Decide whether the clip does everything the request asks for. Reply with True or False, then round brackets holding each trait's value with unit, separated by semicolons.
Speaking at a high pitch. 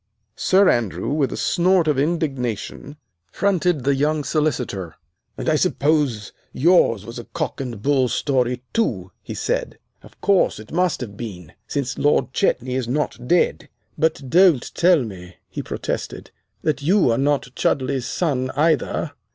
False (140 Hz)